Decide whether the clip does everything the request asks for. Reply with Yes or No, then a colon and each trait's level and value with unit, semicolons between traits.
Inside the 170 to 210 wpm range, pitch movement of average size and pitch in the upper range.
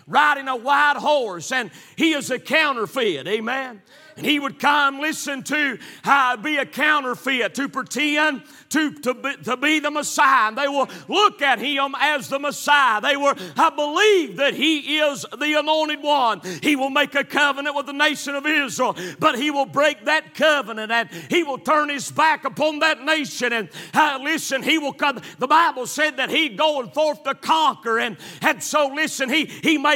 No: average, 190 wpm; narrow, 2.3 semitones; very high, 285 Hz